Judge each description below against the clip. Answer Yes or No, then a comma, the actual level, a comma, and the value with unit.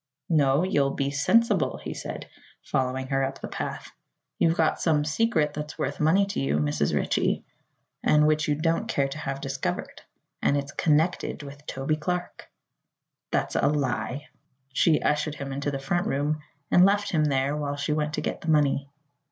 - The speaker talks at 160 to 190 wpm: Yes, average, 175 wpm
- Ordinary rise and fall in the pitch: No, narrow, 2.2 semitones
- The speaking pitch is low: No, medium, 150 Hz